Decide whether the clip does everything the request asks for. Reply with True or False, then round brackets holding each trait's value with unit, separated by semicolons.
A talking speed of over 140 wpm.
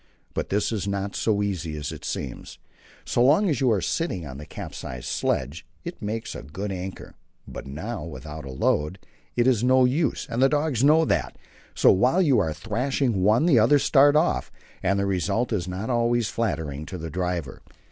True (195 wpm)